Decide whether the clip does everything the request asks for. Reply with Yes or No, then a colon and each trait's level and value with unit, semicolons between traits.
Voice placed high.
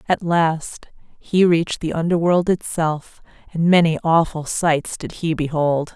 No: medium, 165 Hz